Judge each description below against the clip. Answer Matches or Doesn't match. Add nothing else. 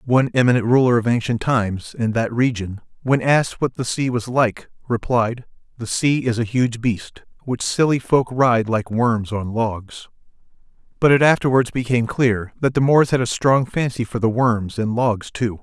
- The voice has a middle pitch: Doesn't match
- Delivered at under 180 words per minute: Doesn't match